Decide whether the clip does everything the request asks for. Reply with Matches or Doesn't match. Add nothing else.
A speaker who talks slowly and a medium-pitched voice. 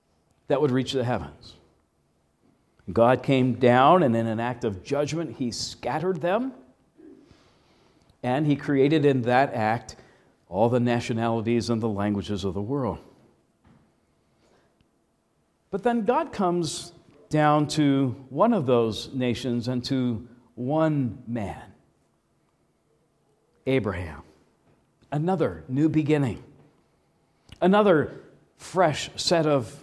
Doesn't match